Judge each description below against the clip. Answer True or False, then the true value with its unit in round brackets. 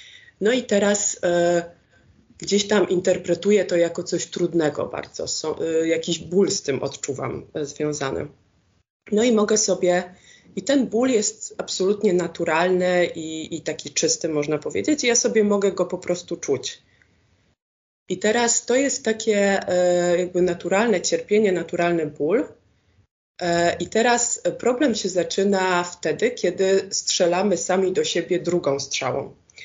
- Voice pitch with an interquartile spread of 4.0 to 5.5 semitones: False (3.5 semitones)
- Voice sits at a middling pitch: True (180 Hz)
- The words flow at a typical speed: True (140 wpm)